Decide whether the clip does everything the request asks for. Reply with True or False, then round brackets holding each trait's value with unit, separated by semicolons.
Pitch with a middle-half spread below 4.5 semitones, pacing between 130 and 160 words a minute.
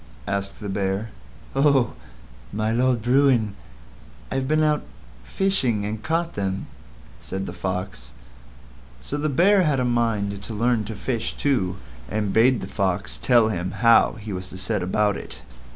False (4.8 semitones; 155 wpm)